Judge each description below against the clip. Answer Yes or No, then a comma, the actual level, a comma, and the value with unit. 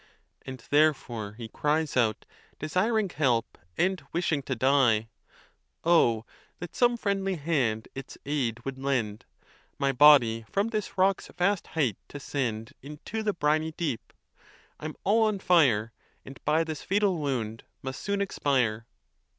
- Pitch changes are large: Yes, wide, 6.8 semitones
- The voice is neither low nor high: Yes, medium, 145 Hz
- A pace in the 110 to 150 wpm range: Yes, average, 140 wpm